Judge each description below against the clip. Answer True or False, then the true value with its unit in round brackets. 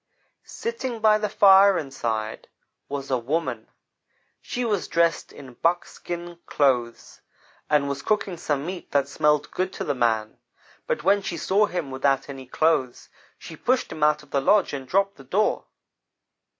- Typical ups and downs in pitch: False (6.1 semitones)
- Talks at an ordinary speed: True (160 wpm)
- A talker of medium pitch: True (150 Hz)